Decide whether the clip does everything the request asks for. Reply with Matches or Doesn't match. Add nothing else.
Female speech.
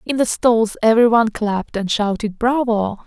Matches